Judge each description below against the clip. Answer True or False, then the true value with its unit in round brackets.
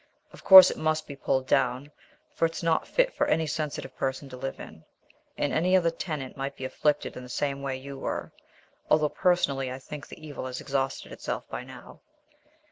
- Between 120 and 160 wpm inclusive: False (200 wpm)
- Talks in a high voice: False (140 Hz)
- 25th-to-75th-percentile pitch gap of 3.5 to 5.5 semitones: False (3.0 semitones)